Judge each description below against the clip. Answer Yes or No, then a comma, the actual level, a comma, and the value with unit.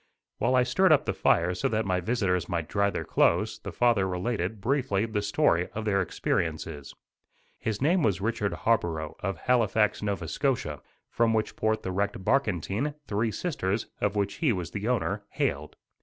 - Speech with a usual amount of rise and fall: Yes, average, 4.0 semitones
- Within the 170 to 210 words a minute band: Yes, average, 175 wpm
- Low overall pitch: Yes, low, 105 Hz